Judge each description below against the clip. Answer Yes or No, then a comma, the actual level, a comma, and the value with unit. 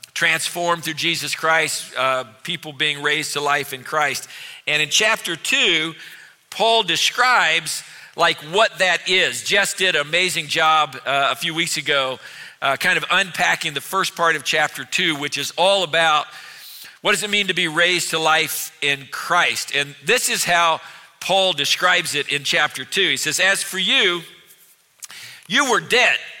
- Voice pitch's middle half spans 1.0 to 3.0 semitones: No, average, 3.6 semitones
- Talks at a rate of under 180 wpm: Yes, average, 170 wpm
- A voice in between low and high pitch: Yes, medium, 160 Hz